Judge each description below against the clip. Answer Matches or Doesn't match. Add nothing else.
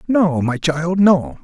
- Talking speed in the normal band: Matches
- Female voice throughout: Doesn't match